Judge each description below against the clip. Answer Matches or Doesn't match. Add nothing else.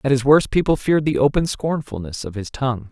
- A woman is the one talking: Doesn't match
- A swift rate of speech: Matches